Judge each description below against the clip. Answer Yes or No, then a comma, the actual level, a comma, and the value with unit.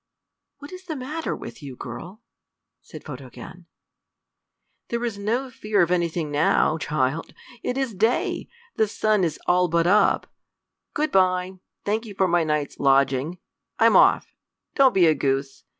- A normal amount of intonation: No, wide, 6.4 semitones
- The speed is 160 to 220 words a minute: No, average, 150 wpm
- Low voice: No, medium, 185 Hz